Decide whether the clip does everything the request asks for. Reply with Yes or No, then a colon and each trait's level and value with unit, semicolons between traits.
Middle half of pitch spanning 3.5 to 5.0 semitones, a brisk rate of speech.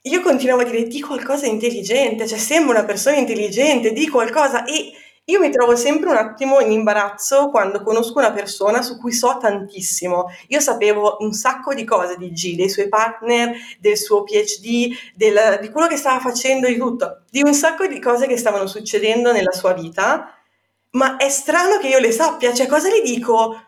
Yes: average, 4.5 semitones; fast, 195 wpm